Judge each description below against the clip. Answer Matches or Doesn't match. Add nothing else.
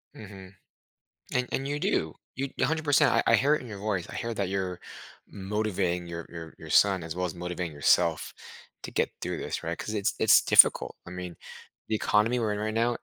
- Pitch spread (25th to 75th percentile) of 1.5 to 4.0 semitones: Doesn't match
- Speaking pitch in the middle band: Doesn't match